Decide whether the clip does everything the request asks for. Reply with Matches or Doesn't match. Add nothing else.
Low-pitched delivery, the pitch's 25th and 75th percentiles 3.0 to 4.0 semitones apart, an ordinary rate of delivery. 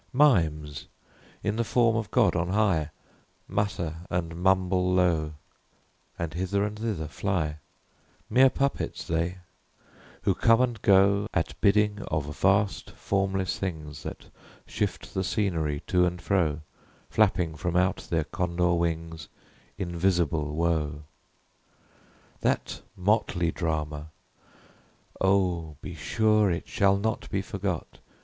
Doesn't match